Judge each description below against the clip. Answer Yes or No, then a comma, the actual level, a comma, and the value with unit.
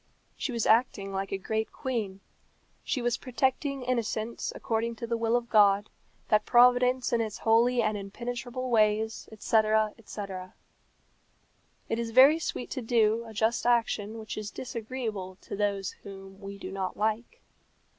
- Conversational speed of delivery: Yes, average, 155 wpm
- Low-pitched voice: No, high, 225 Hz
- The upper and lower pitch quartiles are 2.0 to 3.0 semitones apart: Yes, average, 2.7 semitones